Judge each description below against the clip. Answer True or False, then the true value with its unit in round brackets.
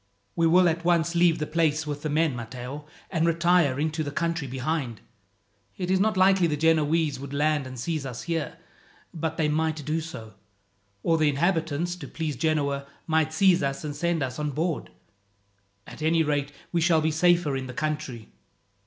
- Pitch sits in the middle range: True (155 Hz)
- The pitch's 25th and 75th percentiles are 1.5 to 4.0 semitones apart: True (2.7 semitones)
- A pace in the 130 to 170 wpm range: False (185 wpm)